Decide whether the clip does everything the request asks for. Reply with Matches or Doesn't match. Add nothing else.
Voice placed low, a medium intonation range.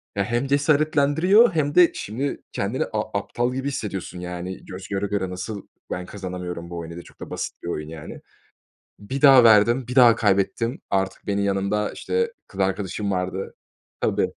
Doesn't match